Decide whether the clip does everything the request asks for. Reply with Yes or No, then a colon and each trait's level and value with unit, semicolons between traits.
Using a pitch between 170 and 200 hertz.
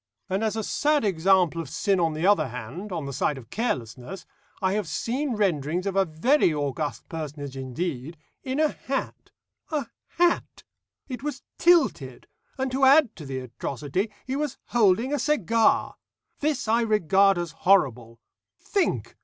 Yes: high, 190 Hz